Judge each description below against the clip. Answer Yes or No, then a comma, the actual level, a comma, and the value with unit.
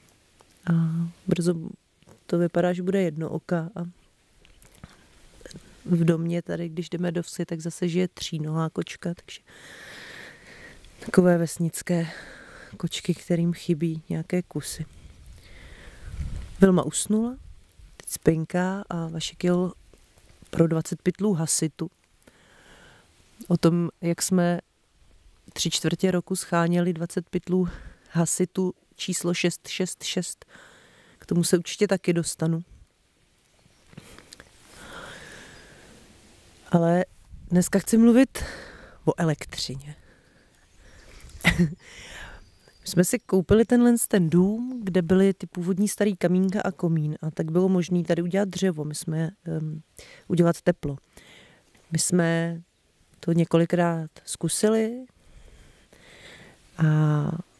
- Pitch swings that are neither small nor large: No, narrow, 2.2 semitones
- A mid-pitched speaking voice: Yes, medium, 175 Hz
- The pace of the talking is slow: Yes, slow, 100 wpm